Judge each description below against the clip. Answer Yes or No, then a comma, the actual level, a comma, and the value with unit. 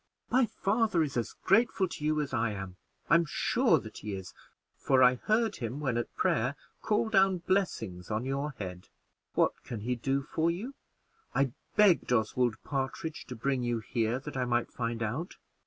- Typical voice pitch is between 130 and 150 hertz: Yes, low, 135 Hz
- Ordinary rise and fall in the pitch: No, wide, 6.6 semitones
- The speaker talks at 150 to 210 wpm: Yes, average, 180 wpm